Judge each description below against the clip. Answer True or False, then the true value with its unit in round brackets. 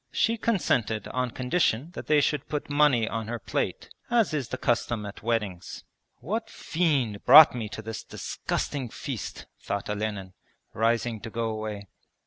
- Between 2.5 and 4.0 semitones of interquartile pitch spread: False (5.3 semitones)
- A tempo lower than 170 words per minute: True (155 wpm)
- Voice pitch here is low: True (120 Hz)